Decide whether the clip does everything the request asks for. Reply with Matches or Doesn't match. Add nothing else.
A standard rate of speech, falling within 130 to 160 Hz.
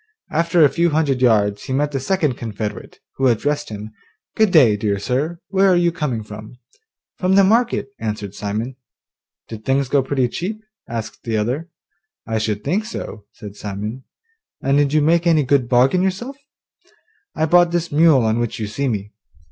Matches